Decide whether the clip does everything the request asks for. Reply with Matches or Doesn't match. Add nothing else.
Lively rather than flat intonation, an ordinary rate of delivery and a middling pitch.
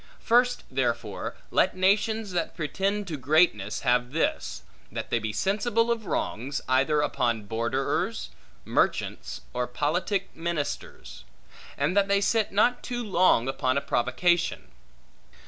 Doesn't match